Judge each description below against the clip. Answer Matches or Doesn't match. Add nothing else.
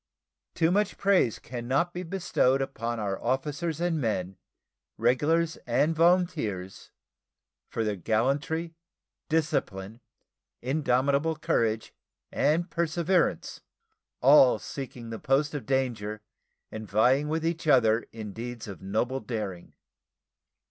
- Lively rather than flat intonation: Matches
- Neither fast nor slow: Doesn't match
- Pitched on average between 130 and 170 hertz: Matches